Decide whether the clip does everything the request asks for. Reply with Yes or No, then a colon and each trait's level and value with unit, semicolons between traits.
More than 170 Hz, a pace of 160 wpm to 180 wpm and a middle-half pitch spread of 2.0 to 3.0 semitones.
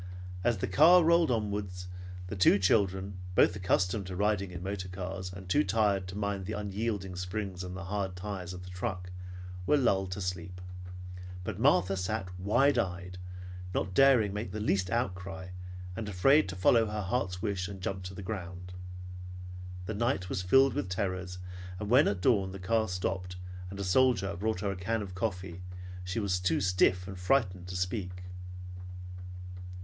No: very low, 95 Hz; average, 175 wpm; narrow, 2.5 semitones